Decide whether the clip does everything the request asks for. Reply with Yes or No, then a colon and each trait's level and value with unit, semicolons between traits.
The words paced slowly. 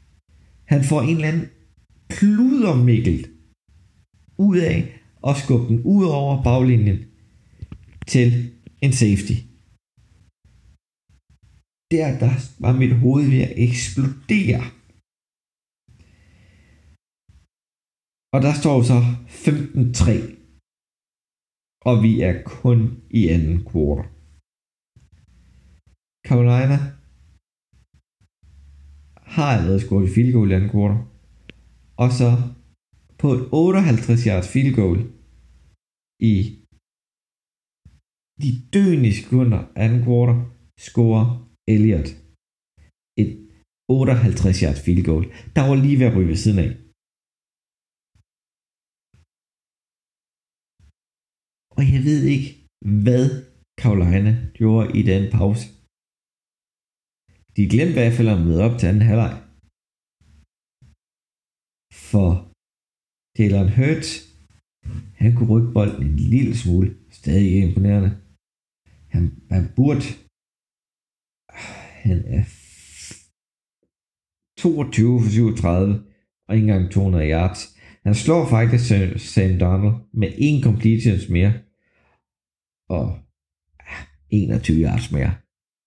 Yes: slow, 95 wpm